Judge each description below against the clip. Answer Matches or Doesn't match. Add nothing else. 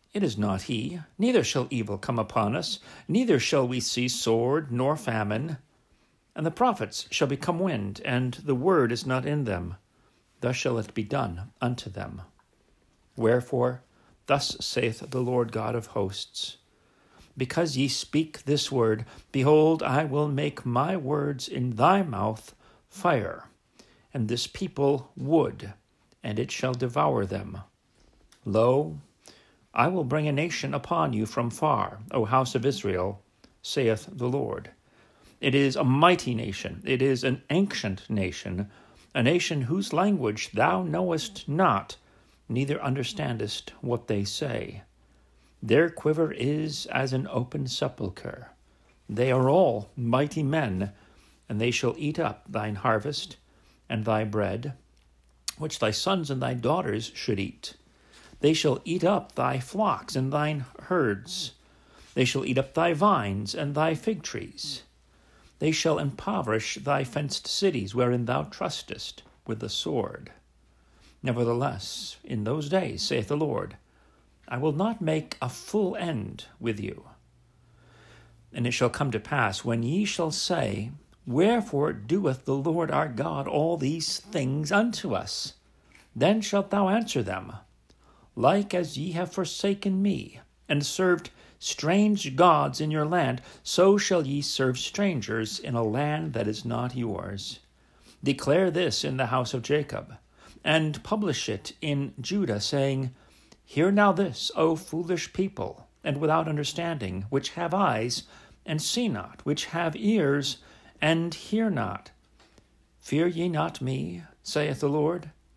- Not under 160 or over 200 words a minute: Doesn't match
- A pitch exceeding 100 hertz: Matches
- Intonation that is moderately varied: Doesn't match